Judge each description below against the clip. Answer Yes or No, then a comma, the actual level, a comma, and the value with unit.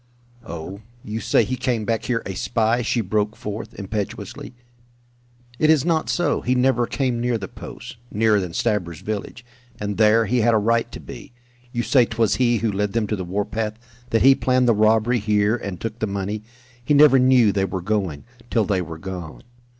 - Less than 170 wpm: No, average, 195 wpm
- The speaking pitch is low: Yes, low, 110 Hz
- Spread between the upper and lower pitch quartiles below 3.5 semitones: Yes, average, 3.0 semitones